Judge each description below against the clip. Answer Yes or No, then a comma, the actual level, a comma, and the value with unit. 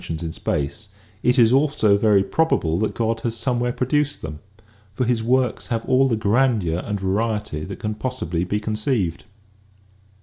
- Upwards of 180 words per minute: No, average, 165 wpm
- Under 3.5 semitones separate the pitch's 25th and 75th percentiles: No, average, 4.3 semitones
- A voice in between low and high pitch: No, low, 110 Hz